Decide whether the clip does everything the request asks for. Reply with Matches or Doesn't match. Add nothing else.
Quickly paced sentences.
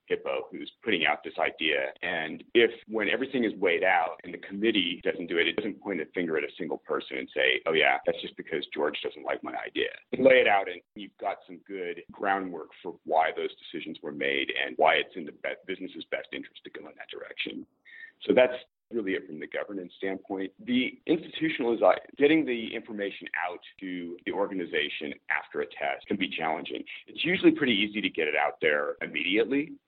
Matches